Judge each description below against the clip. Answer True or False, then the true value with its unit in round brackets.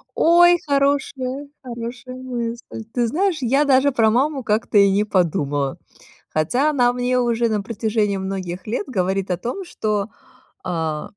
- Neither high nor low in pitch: False (235 Hz)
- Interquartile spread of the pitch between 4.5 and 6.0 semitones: True (5.1 semitones)